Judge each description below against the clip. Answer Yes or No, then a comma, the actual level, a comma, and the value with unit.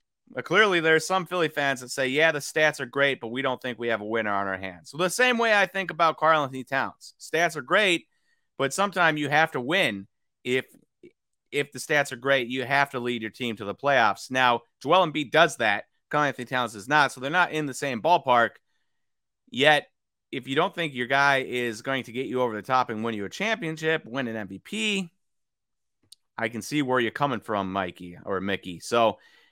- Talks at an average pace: No, fast, 220 wpm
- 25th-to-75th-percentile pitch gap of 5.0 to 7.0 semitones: Yes, wide, 5.4 semitones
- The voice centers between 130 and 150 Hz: Yes, low, 135 Hz